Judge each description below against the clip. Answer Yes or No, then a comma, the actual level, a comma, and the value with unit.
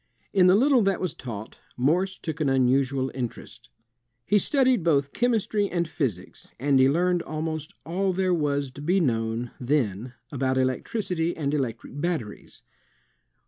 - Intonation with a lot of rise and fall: Yes, wide, 5.7 semitones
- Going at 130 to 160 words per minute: Yes, average, 145 wpm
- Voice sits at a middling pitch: Yes, medium, 150 Hz